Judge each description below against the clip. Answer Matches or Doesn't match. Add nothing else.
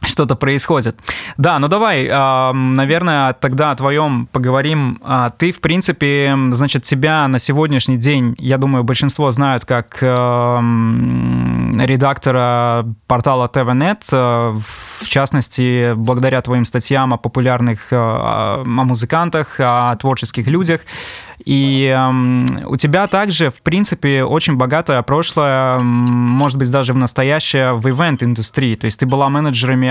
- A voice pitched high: Doesn't match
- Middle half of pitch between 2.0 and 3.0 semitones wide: Matches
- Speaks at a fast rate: Doesn't match